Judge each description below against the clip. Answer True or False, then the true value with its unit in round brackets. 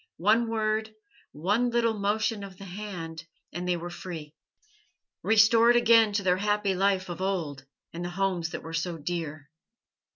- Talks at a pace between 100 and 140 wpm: False (160 wpm)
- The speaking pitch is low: False (195 Hz)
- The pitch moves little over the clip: False (3.9 semitones)